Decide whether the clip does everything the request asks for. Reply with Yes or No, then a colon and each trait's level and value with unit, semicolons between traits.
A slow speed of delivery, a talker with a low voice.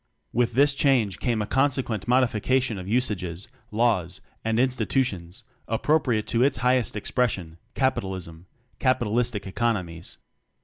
Yes: slow, 105 wpm; low, 115 Hz